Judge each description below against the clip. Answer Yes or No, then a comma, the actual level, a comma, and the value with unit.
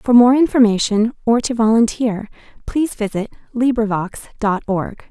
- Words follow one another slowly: Yes, slow, 130 wpm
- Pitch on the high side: Yes, high, 225 Hz